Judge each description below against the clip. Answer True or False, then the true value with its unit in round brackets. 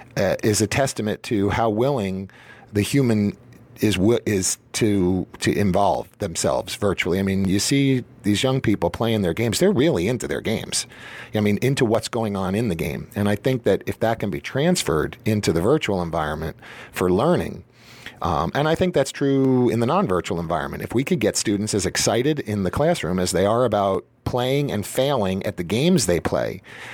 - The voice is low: True (105 Hz)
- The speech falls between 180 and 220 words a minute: True (195 wpm)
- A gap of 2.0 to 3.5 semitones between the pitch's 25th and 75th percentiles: False (5.0 semitones)